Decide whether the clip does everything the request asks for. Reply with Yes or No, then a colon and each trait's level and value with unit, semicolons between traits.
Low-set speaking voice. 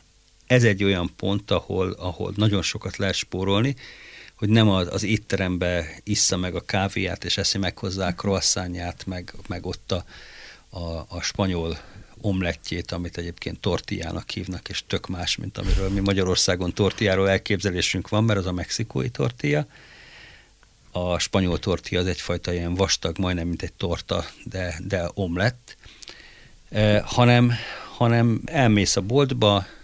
Yes: very low, 95 Hz